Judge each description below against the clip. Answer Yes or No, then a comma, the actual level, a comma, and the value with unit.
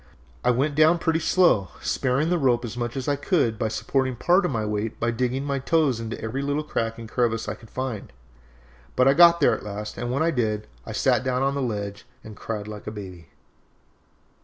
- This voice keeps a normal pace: No, fast, 220 wpm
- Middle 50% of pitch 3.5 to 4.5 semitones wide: Yes, average, 4.2 semitones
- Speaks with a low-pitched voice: Yes, low, 125 Hz